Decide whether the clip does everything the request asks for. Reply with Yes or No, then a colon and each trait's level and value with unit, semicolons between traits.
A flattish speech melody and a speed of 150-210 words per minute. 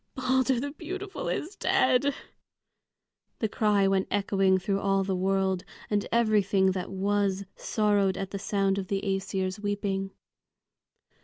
No: narrow, 2.1 semitones; slow, 135 wpm